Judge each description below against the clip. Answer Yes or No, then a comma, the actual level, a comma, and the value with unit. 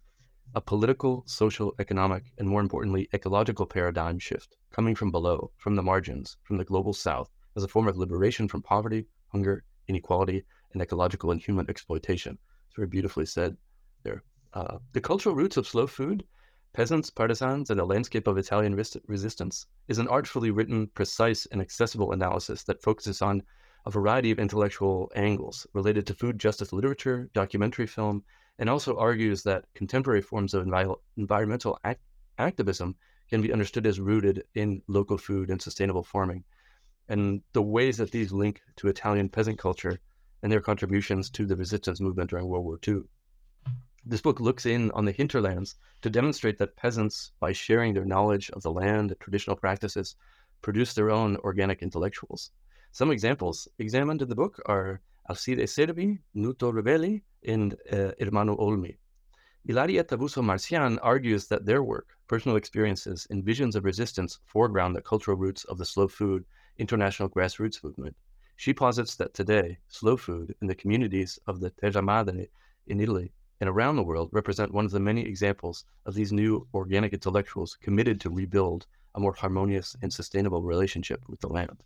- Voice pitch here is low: Yes, low, 100 Hz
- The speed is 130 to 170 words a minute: Yes, average, 165 wpm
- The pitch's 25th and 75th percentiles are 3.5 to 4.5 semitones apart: No, narrow, 2.5 semitones